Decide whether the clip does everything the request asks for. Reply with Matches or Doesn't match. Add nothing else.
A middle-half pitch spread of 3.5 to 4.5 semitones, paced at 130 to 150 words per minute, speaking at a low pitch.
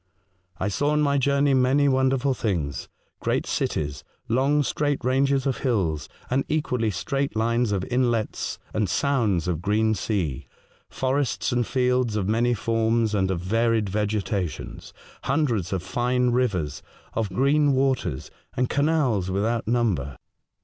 Doesn't match